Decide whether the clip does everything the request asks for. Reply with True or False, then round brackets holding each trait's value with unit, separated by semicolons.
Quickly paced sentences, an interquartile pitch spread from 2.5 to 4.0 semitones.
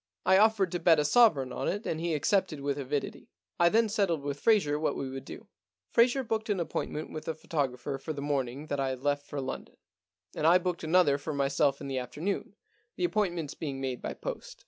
False (215 wpm; 5.3 semitones)